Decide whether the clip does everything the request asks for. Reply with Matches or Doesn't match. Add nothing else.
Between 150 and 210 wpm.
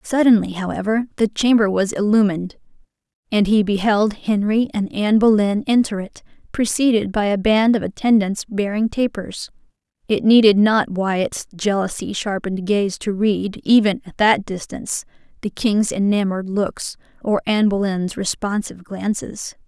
Doesn't match